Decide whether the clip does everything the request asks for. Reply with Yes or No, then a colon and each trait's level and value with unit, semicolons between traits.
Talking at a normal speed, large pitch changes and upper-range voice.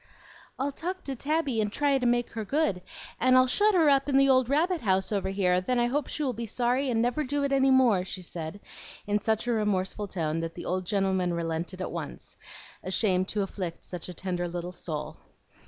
No: fast, 220 wpm; wide, 6.6 semitones; high, 215 Hz